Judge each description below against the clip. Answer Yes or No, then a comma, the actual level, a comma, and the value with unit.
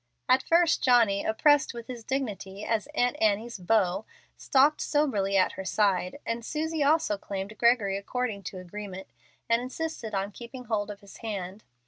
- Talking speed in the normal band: Yes, average, 160 wpm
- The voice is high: Yes, high, 220 Hz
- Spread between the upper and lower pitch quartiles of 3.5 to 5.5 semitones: Yes, average, 4.2 semitones